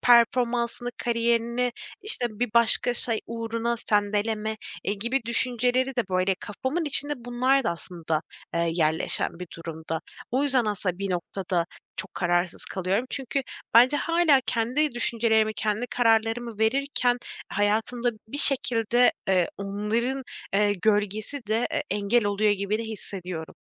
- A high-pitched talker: Yes, high, 225 Hz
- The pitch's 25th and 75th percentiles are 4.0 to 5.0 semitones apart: No, average, 3.5 semitones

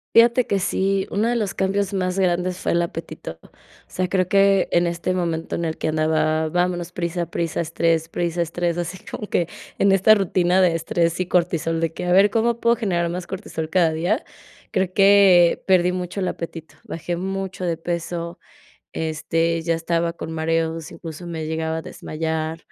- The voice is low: No, medium, 175 Hz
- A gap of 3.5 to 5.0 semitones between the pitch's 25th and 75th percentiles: No, narrow, 2.4 semitones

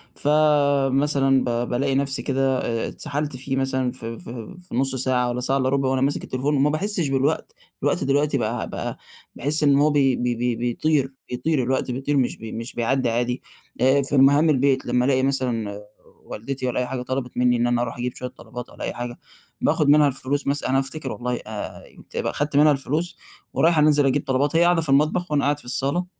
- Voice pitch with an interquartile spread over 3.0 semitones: No, narrow, 2.6 semitones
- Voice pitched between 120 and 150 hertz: Yes, low, 135 Hz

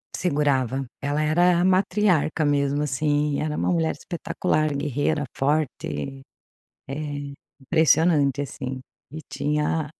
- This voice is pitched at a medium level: Yes, medium, 150 Hz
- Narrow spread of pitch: Yes, narrow, 2.1 semitones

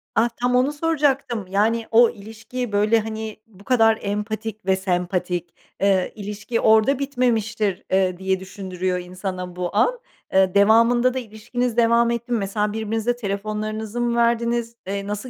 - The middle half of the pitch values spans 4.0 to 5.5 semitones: No, average, 3.1 semitones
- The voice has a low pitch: No, high, 220 Hz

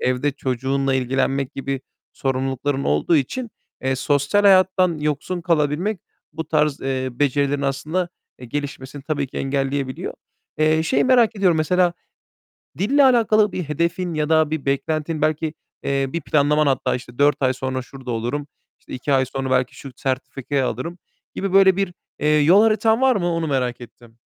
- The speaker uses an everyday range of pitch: Yes, average, 4.5 semitones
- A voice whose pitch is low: No, medium, 145 Hz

